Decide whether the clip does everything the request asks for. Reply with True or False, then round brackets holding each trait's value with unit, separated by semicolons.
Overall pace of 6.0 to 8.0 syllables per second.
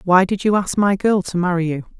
False (5.5 syllables/s)